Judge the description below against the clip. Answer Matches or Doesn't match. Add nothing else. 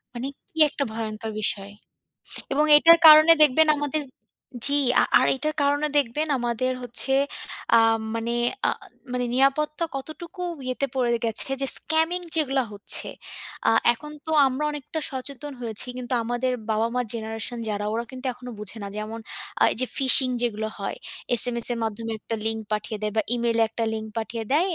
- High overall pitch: Matches